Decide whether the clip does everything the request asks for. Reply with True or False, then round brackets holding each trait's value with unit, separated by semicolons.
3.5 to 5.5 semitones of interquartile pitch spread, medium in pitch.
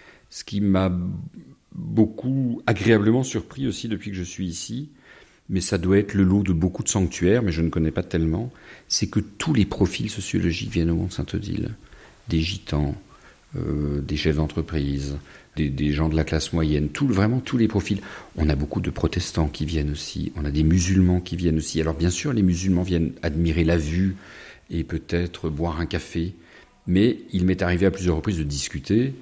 False (3.8 semitones; 90 Hz)